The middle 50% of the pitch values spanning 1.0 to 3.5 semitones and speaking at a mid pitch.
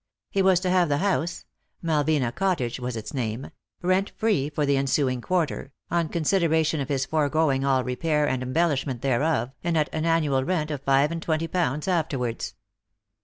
No: average, 3.9 semitones; medium, 150 Hz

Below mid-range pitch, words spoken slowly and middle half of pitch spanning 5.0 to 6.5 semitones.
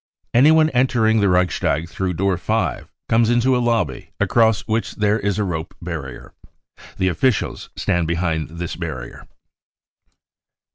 Yes: very low, 95 Hz; slow, 130 wpm; wide, 5.4 semitones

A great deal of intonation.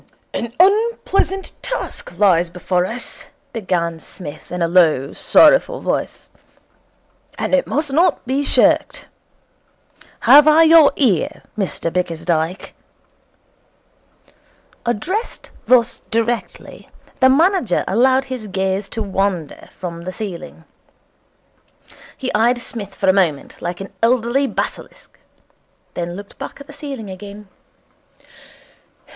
Yes: wide, 7.0 semitones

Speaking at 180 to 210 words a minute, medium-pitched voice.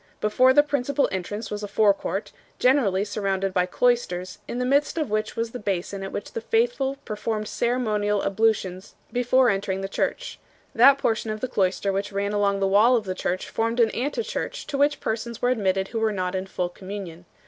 No: average, 200 wpm; high, 210 Hz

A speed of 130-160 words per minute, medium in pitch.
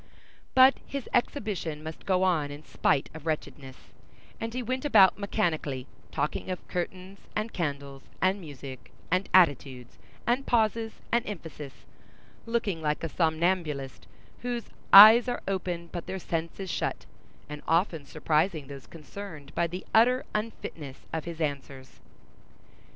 Yes: average, 140 wpm; medium, 170 Hz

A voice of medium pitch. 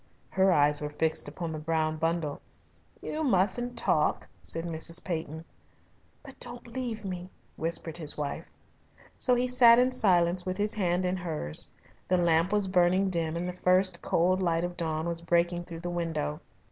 Yes: medium, 175 Hz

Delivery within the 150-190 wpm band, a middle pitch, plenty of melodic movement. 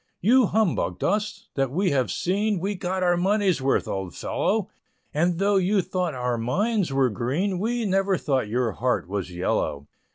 Yes: average, 170 wpm; medium, 180 Hz; wide, 7.9 semitones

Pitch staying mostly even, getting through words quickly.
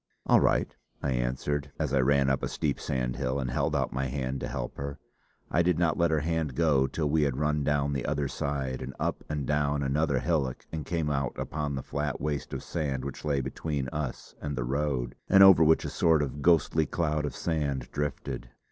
Yes: narrow, 2.2 semitones; fast, 215 wpm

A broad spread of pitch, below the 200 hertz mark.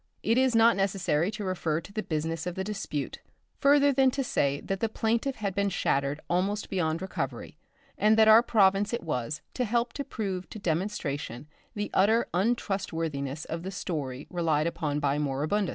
Yes: wide, 5.7 semitones; high, 190 Hz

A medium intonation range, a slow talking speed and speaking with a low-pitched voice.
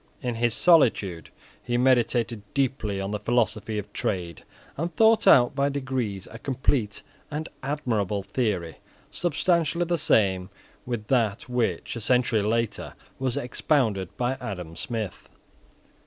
Yes: average, 4.5 semitones; slow, 130 wpm; low, 120 Hz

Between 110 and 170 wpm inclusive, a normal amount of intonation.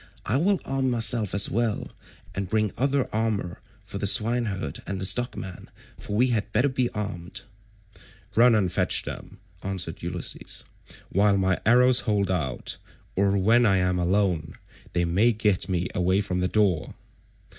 Yes: average, 160 wpm; average, 3.9 semitones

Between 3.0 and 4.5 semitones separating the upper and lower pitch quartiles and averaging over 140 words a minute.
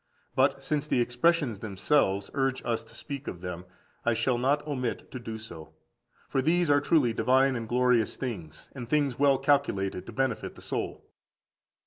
Yes: average, 3.8 semitones; average, 170 wpm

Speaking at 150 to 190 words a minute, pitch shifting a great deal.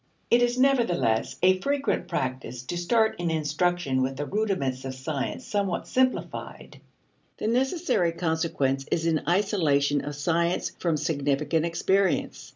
No: slow, 135 wpm; wide, 5.8 semitones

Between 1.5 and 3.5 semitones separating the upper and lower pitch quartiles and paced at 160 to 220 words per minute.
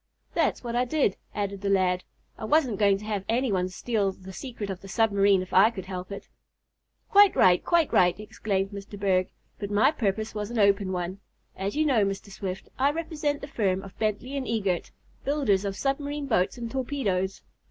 No: average, 4.5 semitones; average, 195 wpm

